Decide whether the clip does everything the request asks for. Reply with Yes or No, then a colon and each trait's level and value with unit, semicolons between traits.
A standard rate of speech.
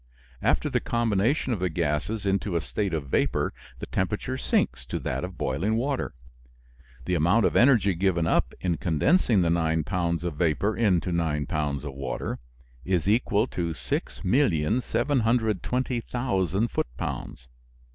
Yes: average, 145 wpm